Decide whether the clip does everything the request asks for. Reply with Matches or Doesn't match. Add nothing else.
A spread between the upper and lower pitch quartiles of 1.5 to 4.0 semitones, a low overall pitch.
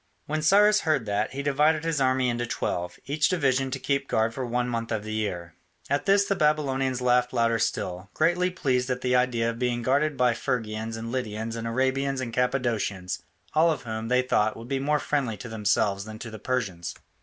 Matches